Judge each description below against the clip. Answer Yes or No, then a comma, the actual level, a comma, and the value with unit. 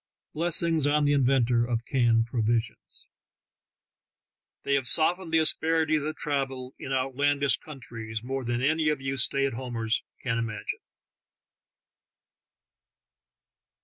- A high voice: No, low, 135 Hz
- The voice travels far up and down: No, average, 4.1 semitones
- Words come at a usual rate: No, slow, 120 wpm